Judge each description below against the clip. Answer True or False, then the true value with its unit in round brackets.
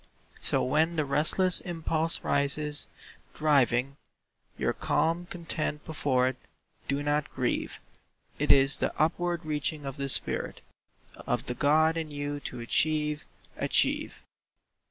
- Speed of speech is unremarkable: False (120 wpm)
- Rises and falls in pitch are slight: True (2.3 semitones)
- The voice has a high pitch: False (150 Hz)